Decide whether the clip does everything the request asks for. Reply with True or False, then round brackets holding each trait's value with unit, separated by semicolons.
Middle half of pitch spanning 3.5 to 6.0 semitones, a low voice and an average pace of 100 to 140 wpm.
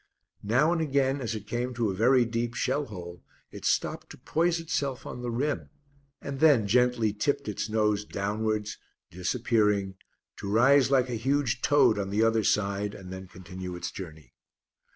False (4.5 semitones; 115 Hz; 175 wpm)